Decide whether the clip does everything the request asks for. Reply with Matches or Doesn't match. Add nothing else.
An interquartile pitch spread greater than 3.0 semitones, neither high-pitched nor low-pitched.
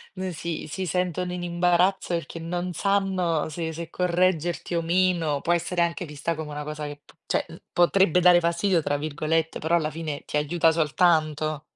Doesn't match